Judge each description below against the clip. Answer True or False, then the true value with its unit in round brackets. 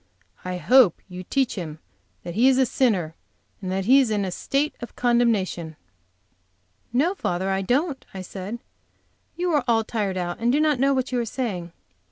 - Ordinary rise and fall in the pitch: False (6.0 semitones)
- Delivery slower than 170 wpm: False (185 wpm)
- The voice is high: True (230 Hz)